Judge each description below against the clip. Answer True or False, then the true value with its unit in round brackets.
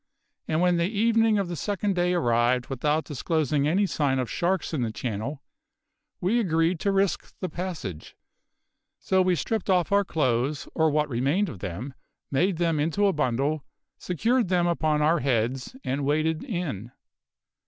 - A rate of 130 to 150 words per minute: False (165 wpm)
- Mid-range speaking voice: True (160 Hz)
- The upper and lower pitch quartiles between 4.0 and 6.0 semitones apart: True (5.2 semitones)